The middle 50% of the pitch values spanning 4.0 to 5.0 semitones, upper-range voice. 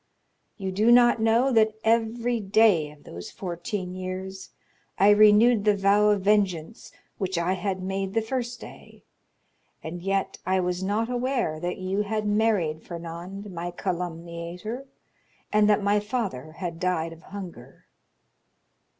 No: average, 3.5 semitones; high, 195 Hz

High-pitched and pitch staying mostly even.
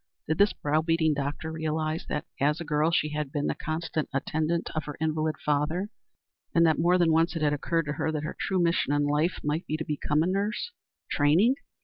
No: medium, 155 Hz; narrow, 1.9 semitones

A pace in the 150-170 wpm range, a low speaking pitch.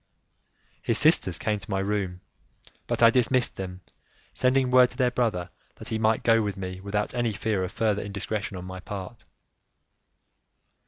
Yes: average, 165 wpm; low, 105 Hz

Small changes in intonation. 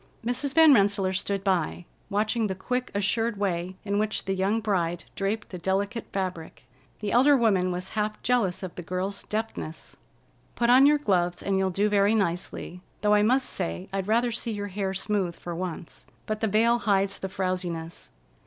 No: average, 3.1 semitones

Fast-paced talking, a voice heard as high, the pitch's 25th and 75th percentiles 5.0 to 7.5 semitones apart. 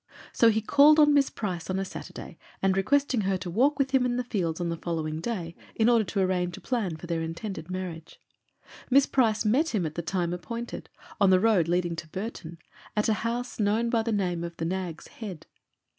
Yes: fast, 220 wpm; high, 195 Hz; average, 5.3 semitones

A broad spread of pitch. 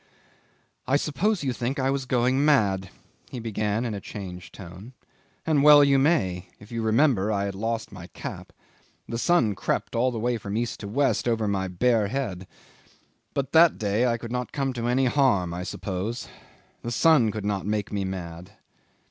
No: average, 4.9 semitones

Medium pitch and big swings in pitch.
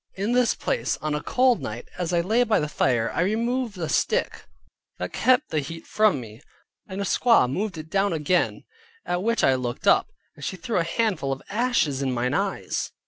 Yes: medium, 175 Hz; wide, 8.1 semitones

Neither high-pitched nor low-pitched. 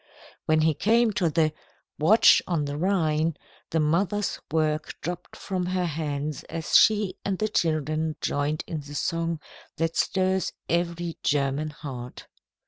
Yes: medium, 160 Hz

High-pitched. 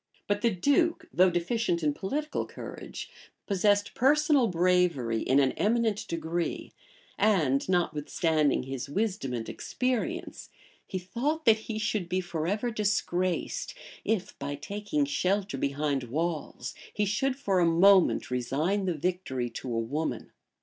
No: medium, 180 Hz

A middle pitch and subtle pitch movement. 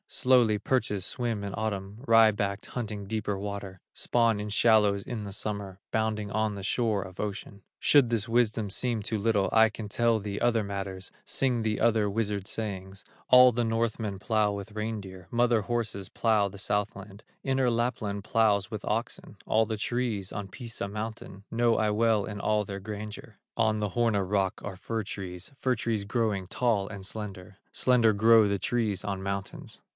No: low, 105 Hz; narrow, 2.2 semitones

